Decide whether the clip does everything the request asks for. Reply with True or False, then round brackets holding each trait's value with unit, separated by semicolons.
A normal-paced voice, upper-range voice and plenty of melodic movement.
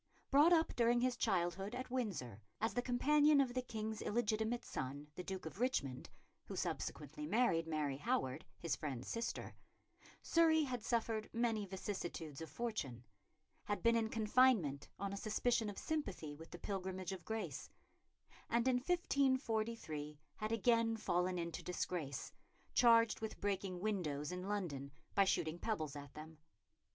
True (150 wpm; 205 Hz; 6.6 semitones)